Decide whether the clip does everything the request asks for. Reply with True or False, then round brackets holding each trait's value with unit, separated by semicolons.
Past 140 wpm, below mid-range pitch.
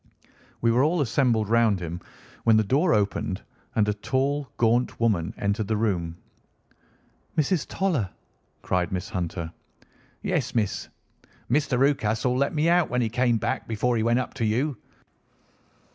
True (150 wpm; 115 Hz)